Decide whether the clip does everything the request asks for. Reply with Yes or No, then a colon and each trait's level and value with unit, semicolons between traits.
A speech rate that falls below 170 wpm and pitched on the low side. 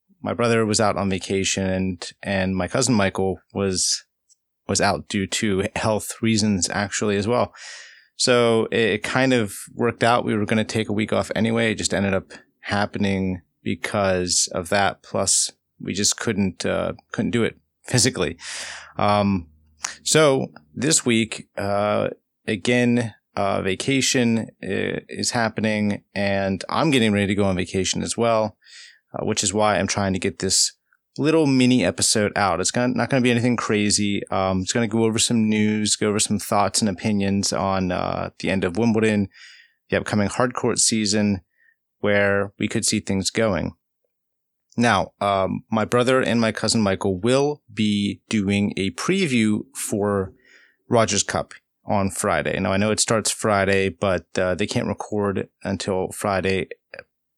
Yes: average, 160 wpm; low, 105 Hz